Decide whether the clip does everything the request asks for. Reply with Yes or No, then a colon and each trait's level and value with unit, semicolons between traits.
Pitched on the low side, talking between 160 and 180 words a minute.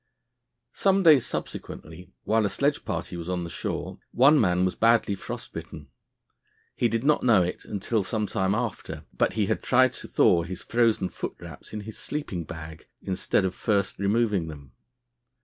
Yes: low, 100 Hz; average, 170 wpm